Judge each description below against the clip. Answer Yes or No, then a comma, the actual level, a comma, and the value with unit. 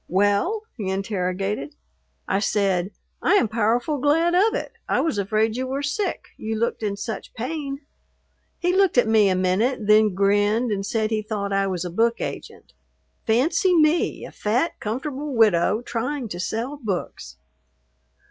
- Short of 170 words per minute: Yes, average, 160 wpm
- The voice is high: Yes, high, 220 Hz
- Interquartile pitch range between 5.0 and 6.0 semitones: Yes, wide, 5.5 semitones